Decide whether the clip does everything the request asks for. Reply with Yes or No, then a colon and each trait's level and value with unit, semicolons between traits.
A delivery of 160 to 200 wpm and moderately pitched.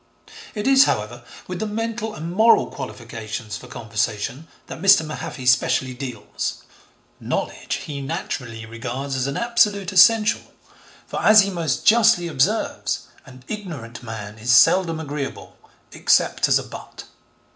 No: slow, 135 wpm; medium, 145 Hz